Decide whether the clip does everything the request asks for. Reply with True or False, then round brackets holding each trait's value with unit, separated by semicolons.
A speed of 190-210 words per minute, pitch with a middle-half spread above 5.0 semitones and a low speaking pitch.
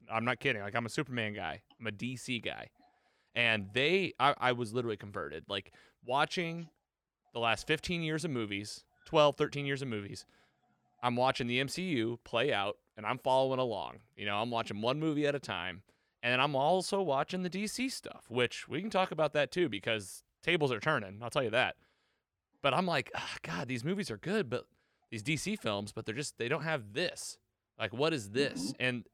True (200 wpm; 5.5 semitones; 125 Hz)